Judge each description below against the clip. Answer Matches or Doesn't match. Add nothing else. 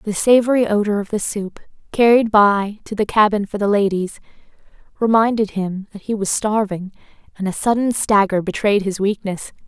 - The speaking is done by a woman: Matches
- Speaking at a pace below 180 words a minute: Matches